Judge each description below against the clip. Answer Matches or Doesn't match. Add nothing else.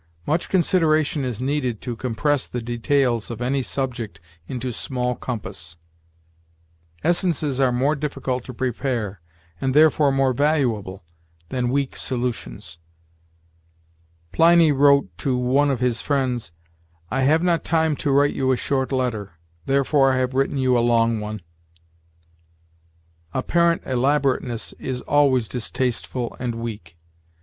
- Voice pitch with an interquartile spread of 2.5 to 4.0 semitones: Matches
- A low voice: Matches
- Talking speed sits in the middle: Doesn't match